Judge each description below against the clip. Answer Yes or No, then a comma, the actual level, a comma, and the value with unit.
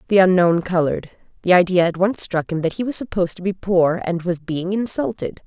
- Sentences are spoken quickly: Yes, fast, 220 wpm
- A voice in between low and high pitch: Yes, medium, 180 Hz